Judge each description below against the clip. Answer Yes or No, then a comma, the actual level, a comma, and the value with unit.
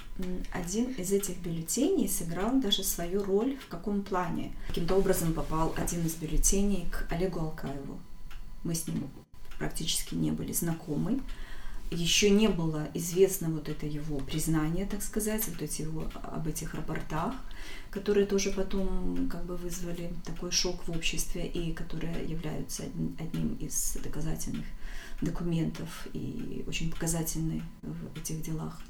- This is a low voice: No, medium, 170 Hz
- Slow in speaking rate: No, average, 135 wpm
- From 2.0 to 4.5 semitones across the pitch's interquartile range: Yes, average, 3.9 semitones